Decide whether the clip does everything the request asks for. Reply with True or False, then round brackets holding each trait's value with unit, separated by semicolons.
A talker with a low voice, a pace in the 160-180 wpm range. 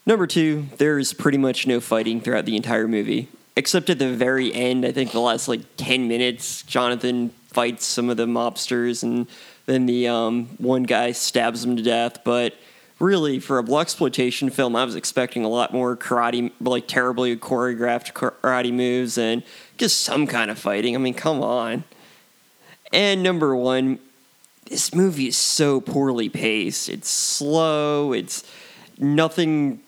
True (125 Hz; 165 wpm)